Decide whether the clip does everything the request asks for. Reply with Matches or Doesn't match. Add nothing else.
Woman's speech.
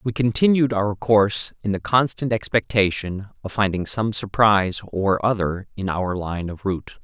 Doesn't match